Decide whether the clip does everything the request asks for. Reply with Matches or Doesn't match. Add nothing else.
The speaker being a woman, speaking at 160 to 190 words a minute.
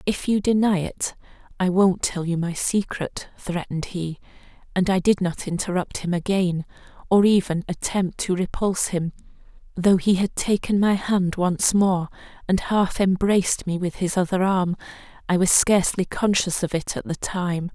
Matches